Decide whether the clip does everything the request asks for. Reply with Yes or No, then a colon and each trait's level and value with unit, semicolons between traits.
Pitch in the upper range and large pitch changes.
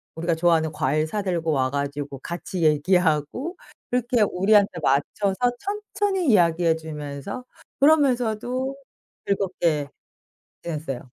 No: medium, 175 Hz; wide, 7.8 semitones